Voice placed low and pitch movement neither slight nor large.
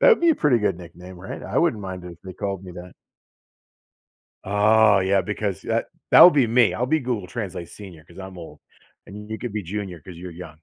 Yes: very low, 95 Hz; average, 3.5 semitones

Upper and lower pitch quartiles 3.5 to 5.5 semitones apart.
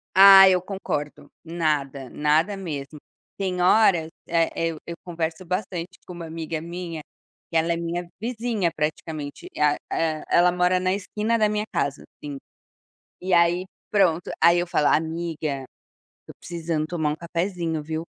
No: narrow, 2.6 semitones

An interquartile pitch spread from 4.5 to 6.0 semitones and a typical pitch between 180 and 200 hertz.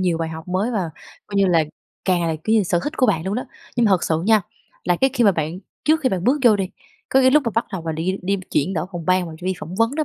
Yes: average, 5.0 semitones; high, 190 Hz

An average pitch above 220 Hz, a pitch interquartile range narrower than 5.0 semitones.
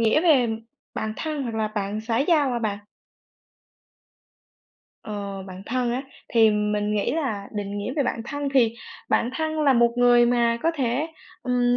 Yes: high, 235 Hz; average, 3.9 semitones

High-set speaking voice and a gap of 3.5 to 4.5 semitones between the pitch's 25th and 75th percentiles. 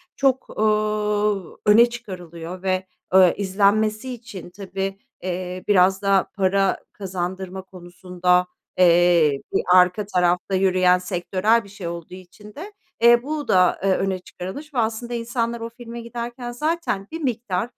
Yes: high, 195 Hz; average, 4.1 semitones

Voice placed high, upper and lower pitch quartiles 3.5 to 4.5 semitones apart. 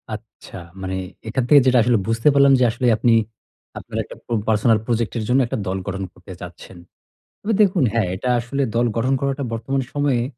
No: low, 120 Hz; average, 3.8 semitones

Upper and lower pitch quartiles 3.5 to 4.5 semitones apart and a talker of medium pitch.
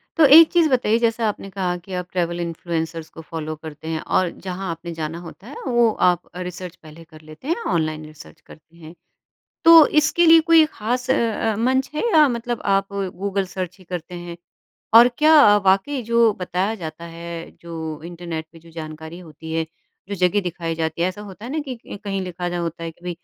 No: average, 5.3 semitones; medium, 180 Hz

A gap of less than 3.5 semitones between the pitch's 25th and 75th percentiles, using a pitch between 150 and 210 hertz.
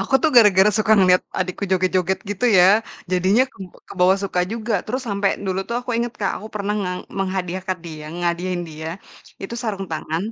Yes: narrow, 2.4 semitones; high, 190 Hz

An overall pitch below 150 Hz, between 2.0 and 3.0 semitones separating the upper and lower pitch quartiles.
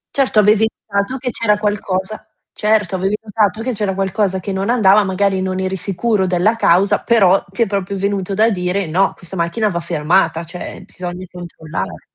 No: high, 195 Hz; narrow, 2.5 semitones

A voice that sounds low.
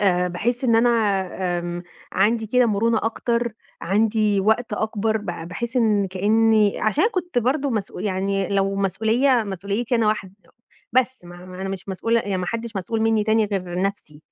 No: high, 215 Hz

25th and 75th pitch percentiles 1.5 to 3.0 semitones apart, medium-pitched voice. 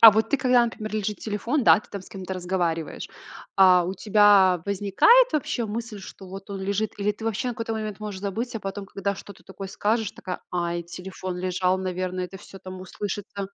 No: narrow, 2.6 semitones; high, 200 Hz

